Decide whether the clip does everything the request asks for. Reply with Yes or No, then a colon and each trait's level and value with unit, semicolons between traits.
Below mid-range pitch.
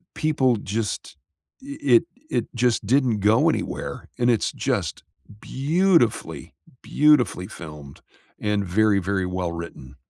Yes: low, 110 Hz